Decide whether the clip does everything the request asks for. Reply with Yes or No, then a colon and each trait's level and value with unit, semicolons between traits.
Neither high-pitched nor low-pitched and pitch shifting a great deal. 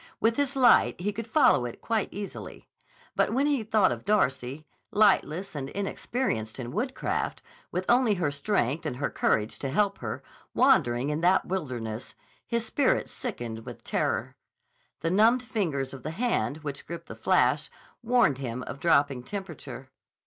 Yes: medium, 175 Hz; wide, 8.5 semitones